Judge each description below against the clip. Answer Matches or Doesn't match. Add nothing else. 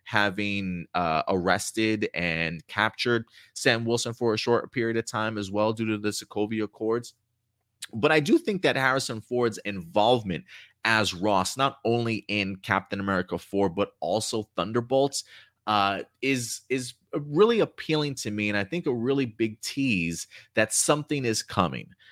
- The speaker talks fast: Doesn't match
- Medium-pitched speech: Doesn't match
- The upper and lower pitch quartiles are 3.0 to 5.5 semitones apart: Matches